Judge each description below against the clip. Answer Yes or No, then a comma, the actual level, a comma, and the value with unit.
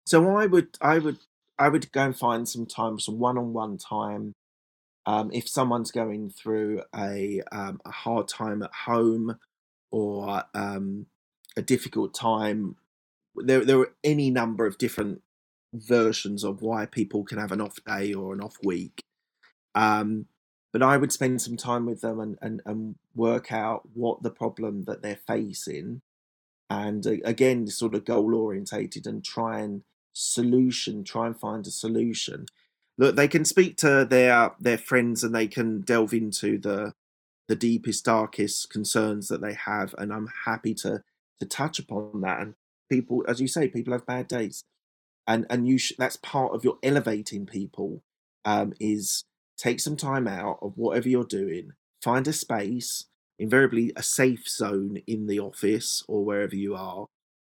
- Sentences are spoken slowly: No, average, 165 wpm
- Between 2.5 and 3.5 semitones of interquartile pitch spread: Yes, average, 3.0 semitones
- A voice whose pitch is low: Yes, low, 115 Hz